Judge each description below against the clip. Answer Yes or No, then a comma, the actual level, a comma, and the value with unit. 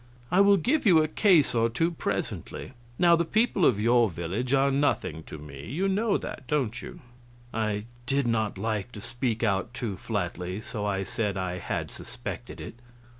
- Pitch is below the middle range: Yes, low, 120 Hz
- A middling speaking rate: Yes, average, 180 wpm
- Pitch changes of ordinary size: No, wide, 7.8 semitones